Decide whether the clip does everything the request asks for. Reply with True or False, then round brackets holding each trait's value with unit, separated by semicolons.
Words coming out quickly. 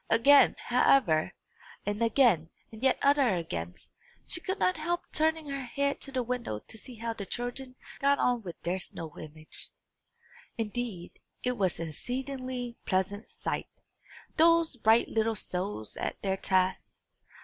False (150 wpm)